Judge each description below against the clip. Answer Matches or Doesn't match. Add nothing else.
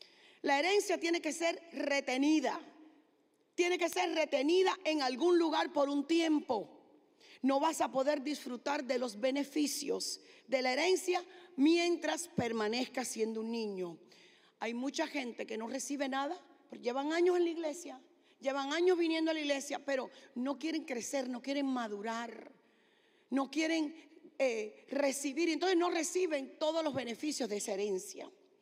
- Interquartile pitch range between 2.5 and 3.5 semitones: Doesn't match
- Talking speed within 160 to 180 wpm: Doesn't match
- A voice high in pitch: Matches